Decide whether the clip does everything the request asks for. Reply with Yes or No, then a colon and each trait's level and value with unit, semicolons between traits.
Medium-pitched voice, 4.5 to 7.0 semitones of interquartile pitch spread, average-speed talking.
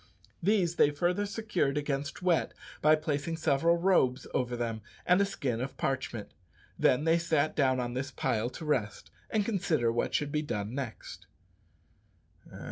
Yes: medium, 145 Hz; average, 5.0 semitones; average, 155 wpm